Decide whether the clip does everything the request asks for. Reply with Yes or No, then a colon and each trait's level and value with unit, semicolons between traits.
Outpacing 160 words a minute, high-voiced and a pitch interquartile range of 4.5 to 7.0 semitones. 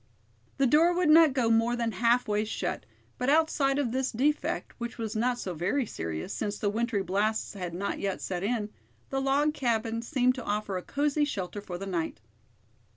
Yes: average, 195 wpm; high, 230 Hz; average, 4.9 semitones